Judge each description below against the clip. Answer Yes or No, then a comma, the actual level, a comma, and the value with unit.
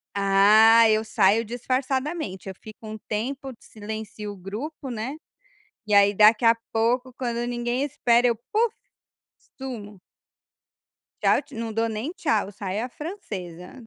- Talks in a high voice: Yes, high, 225 Hz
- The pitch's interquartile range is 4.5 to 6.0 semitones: No, average, 3.4 semitones